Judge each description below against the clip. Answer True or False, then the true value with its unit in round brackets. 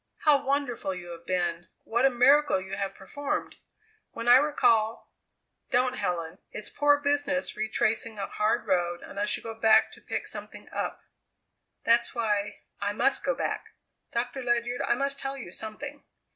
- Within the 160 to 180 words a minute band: True (165 wpm)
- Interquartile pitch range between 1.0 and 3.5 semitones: False (5.2 semitones)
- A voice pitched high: True (230 Hz)